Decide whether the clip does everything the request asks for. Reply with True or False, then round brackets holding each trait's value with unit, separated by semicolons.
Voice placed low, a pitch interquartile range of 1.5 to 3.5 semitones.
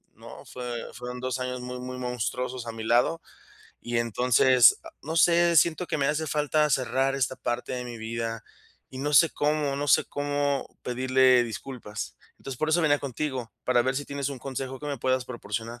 True (130 Hz; 2.7 semitones)